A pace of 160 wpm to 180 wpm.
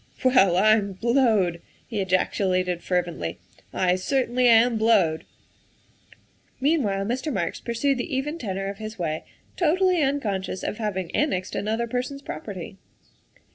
No: average, 140 wpm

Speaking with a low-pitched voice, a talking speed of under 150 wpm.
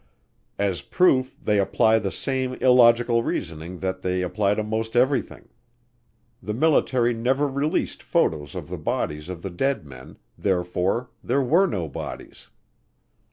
Yes: low, 110 Hz; average, 140 wpm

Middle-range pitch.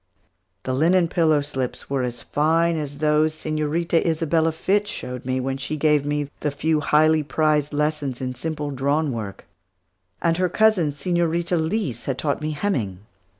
Yes: medium, 150 Hz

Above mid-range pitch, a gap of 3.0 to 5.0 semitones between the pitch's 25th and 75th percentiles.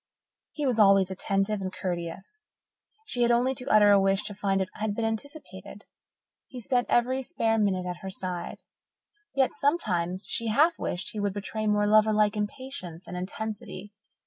Yes: high, 210 Hz; average, 3.8 semitones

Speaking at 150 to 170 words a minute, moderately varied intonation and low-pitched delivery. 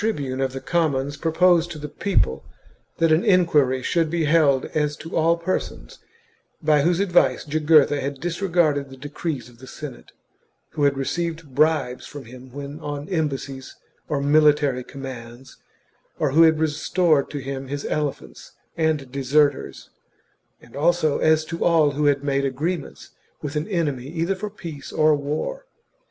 No: average, 160 wpm; average, 3.1 semitones; medium, 150 Hz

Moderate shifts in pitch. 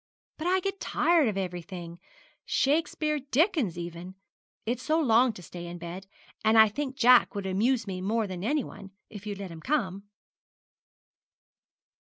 No: wide, 6.8 semitones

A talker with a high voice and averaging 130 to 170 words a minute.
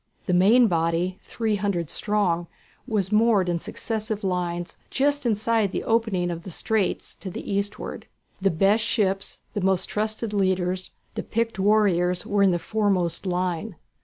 Yes: high, 195 Hz; average, 155 wpm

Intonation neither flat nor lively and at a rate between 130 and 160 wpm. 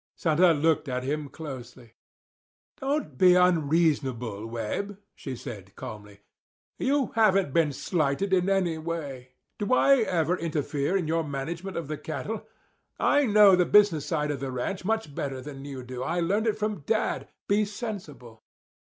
No: wide, 6.3 semitones; average, 155 wpm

